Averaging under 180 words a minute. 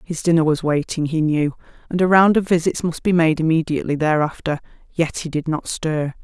No: average, 200 wpm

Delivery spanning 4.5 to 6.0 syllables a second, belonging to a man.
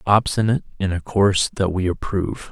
Yes: 5.9 syllables/s; male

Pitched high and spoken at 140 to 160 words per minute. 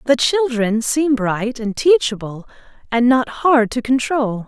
Yes: high, 245 Hz; average, 150 wpm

